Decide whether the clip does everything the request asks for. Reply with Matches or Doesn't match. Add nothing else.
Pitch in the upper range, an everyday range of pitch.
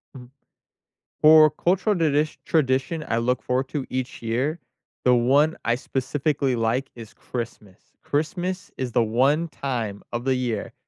Doesn't match